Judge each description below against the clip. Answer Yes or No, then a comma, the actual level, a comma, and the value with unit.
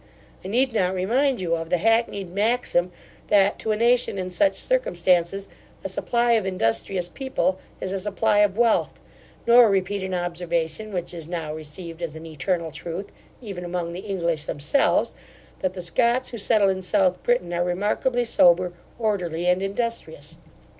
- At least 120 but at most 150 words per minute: No, average, 165 wpm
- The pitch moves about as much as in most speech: Yes, average, 4.1 semitones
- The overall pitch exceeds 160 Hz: Yes, high, 190 Hz